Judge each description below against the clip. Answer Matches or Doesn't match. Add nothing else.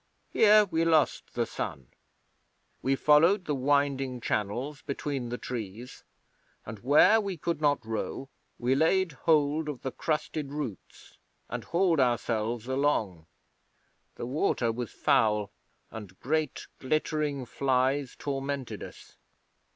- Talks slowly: Matches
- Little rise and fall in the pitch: Doesn't match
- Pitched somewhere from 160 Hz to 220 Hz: Doesn't match